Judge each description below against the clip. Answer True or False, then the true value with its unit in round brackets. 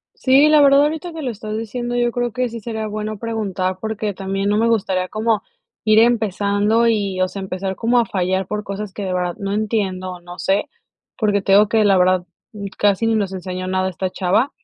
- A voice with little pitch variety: False (3.2 semitones)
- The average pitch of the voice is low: False (210 Hz)